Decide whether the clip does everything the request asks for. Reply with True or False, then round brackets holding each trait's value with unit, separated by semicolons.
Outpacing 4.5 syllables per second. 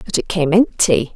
True (4.9 syllables/s)